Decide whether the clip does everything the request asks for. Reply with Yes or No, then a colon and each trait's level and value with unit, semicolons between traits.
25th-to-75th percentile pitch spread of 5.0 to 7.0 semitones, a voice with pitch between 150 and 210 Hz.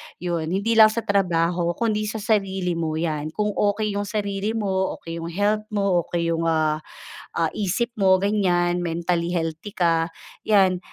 No: average, 3.6 semitones; medium, 185 Hz